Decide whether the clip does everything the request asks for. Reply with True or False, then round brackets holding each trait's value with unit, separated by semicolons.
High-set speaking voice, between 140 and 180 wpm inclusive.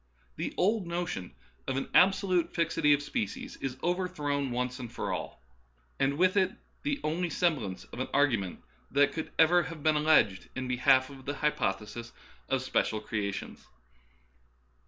False (145 Hz; 160 wpm)